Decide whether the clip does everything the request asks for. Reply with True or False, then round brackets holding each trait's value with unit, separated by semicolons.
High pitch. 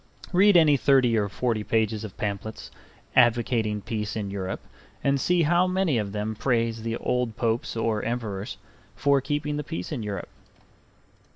False (115 Hz)